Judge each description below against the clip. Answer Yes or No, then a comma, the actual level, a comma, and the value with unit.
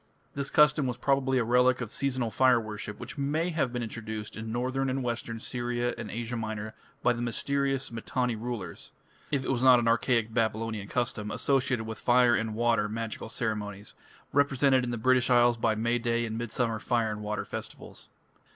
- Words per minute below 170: No, average, 185 wpm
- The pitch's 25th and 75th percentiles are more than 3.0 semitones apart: No, narrow, 2.5 semitones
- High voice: No, low, 120 Hz